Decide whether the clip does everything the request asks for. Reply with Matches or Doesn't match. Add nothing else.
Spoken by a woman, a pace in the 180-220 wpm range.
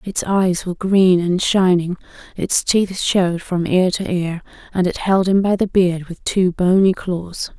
Matches